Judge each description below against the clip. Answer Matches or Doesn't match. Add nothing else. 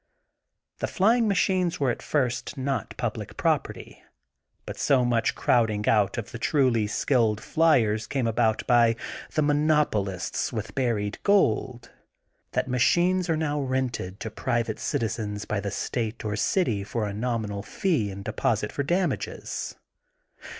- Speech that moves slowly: Doesn't match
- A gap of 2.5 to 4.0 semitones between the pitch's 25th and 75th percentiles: Doesn't match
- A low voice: Matches